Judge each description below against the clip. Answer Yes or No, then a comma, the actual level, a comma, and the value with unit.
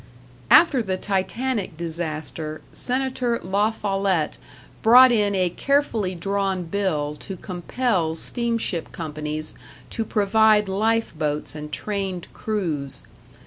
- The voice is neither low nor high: No, high, 195 Hz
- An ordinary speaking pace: No, slow, 105 wpm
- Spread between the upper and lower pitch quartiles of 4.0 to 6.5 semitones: Yes, average, 5.2 semitones